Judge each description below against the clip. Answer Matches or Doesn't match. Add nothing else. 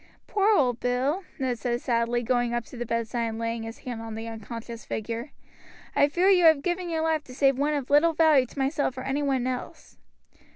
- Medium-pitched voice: Doesn't match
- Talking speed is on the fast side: Matches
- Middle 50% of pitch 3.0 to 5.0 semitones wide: Matches